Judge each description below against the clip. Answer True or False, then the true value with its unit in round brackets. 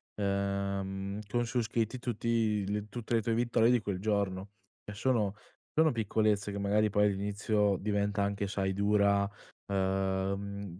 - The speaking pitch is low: True (100 Hz)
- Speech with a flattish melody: True (1.8 semitones)